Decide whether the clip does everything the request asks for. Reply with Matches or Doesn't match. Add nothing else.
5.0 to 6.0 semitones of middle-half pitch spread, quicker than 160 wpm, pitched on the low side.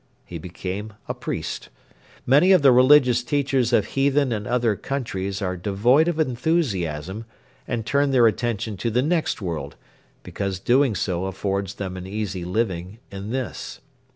Doesn't match